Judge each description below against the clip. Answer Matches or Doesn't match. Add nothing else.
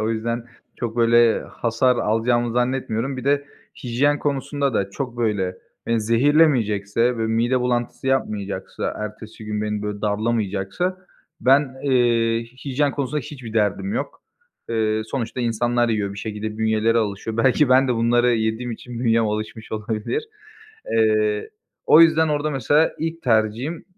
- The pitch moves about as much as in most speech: Matches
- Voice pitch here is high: Doesn't match